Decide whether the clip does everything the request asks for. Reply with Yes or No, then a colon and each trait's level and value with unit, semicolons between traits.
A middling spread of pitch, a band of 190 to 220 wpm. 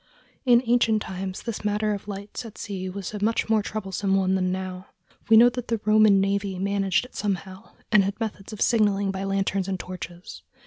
No: narrow, 2.1 semitones; average, 195 wpm